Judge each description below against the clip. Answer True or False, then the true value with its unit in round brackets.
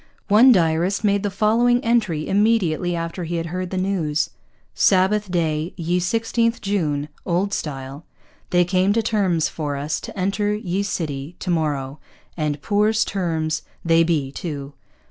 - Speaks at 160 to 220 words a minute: False (150 wpm)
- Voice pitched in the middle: True (175 Hz)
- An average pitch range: True (4.4 semitones)